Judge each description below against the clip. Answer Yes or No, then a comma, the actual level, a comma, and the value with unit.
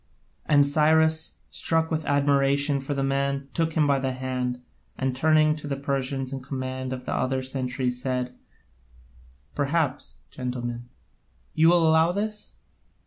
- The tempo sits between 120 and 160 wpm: Yes, average, 140 wpm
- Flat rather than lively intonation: No, average, 3.0 semitones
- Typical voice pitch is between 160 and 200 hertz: No, medium, 140 Hz